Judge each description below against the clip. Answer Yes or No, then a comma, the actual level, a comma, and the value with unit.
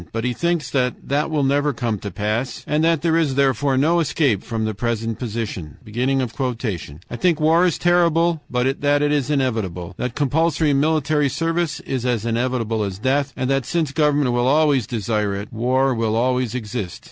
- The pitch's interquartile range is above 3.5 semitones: Yes, average, 4.6 semitones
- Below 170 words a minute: No, average, 180 wpm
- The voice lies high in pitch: No, low, 130 Hz